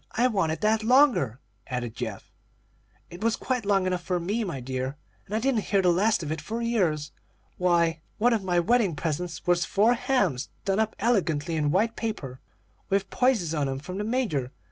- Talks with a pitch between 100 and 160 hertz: No, medium, 185 Hz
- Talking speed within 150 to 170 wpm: No, average, 190 wpm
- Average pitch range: No, wide, 6.0 semitones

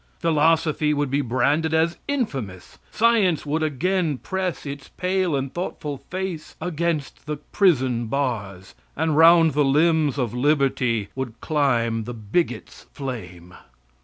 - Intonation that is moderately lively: Yes, average, 4.6 semitones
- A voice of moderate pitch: Yes, medium, 145 Hz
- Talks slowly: Yes, slow, 130 wpm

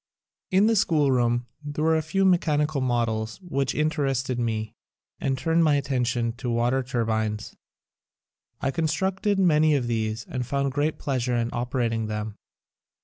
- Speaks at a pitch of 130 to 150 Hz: Yes, low, 135 Hz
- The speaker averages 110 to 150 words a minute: Yes, average, 145 wpm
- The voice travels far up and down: No, average, 4.7 semitones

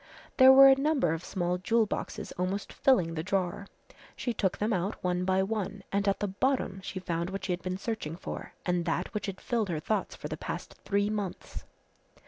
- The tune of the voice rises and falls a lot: No, average, 3.1 semitones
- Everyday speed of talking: No, fast, 210 wpm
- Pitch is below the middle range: No, high, 195 Hz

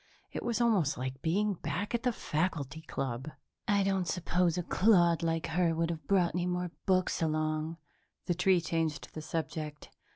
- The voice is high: No, medium, 170 Hz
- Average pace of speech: Yes, average, 170 wpm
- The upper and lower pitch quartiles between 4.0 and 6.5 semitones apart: No, average, 2.9 semitones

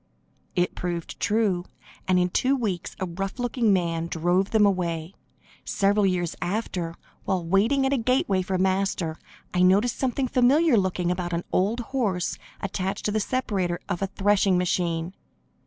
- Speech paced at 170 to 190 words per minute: No, average, 155 wpm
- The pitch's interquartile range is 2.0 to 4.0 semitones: Yes, average, 3.5 semitones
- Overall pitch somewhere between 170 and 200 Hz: Yes, high, 190 Hz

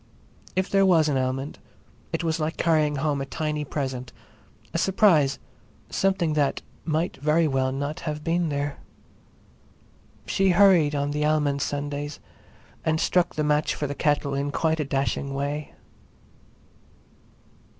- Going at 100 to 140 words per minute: Yes, slow, 135 wpm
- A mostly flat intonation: Yes, narrow, 2.2 semitones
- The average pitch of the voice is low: No, medium, 150 Hz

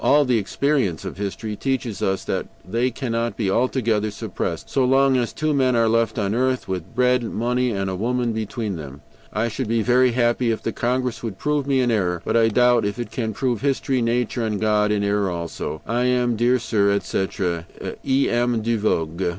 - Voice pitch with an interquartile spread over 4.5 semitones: No, average, 3.3 semitones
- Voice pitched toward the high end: No, low, 115 Hz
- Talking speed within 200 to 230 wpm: Yes, fast, 205 wpm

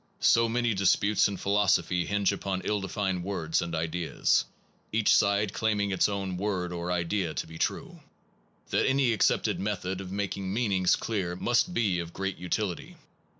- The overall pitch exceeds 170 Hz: No, very low, 95 Hz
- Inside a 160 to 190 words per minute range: Yes, average, 165 wpm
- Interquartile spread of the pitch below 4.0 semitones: Yes, average, 2.7 semitones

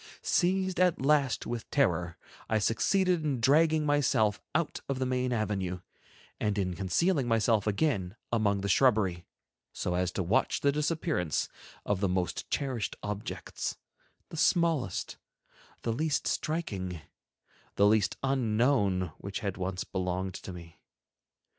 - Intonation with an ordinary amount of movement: No, wide, 7.3 semitones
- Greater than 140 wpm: No, slow, 135 wpm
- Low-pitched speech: Yes, low, 110 Hz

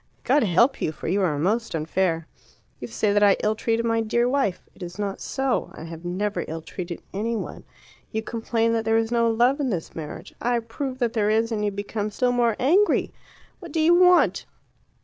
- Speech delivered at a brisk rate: Yes, fast, 210 wpm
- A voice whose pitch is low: No, high, 225 Hz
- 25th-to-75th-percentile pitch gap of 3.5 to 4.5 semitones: Yes, average, 3.9 semitones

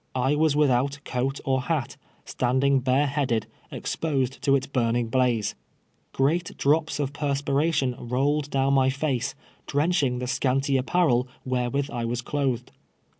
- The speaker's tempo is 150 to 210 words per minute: No, average, 140 wpm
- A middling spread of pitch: No, narrow, 2.3 semitones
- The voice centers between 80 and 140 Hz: Yes, low, 135 Hz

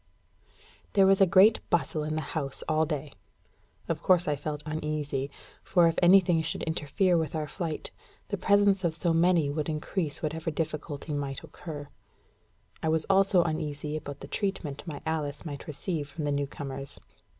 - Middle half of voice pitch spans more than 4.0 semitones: No, average, 2.9 semitones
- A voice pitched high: No, medium, 155 Hz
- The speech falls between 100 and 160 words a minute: No, average, 170 wpm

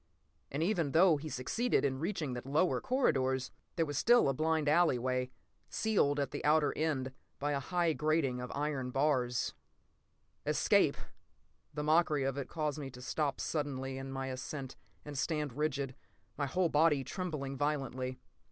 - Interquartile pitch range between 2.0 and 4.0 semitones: Yes, average, 3.0 semitones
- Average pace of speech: Yes, average, 160 wpm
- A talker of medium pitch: Yes, medium, 145 Hz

